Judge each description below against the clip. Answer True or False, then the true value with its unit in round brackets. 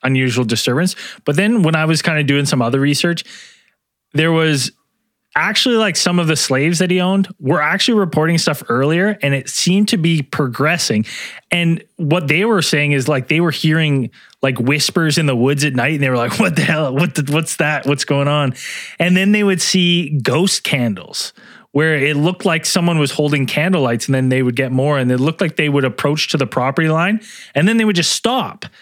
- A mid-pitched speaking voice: True (155 Hz)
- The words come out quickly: True (220 wpm)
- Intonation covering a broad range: False (4.2 semitones)